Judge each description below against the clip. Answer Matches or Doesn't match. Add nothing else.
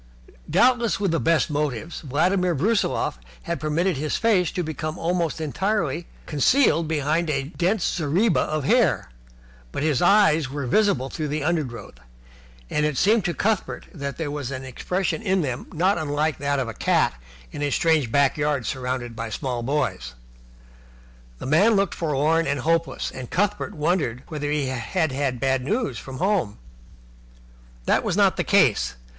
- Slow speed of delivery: Doesn't match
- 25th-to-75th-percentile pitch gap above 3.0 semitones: Matches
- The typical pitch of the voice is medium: Matches